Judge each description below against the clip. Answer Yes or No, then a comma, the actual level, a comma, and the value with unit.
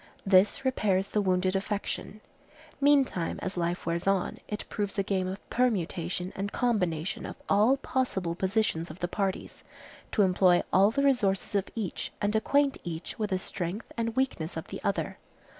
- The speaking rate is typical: Yes, average, 165 wpm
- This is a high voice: Yes, high, 195 Hz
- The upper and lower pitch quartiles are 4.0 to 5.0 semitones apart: No, average, 3.2 semitones